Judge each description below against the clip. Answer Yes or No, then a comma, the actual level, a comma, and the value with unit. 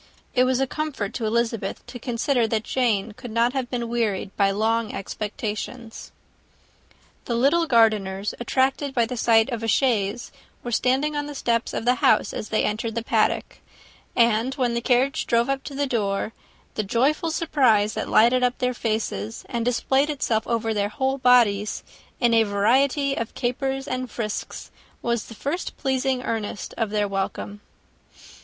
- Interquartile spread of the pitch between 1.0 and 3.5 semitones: Yes, average, 3.1 semitones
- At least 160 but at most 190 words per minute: Yes, average, 170 wpm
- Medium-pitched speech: No, high, 235 Hz